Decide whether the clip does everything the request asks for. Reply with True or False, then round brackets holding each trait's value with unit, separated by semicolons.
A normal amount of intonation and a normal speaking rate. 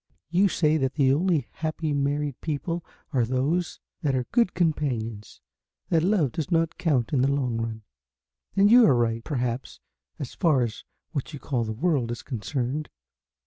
True (4.8 semitones; 170 wpm)